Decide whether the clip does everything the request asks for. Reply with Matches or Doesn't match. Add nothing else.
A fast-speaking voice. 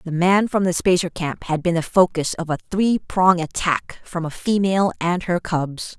Matches